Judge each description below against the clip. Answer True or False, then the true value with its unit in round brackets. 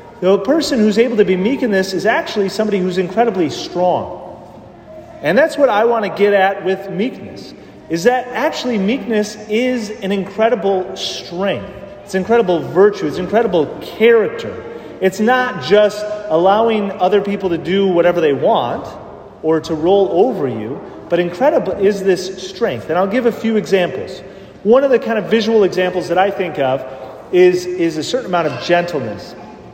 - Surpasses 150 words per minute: True (170 wpm)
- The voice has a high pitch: True (195 Hz)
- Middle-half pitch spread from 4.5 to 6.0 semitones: False (3.8 semitones)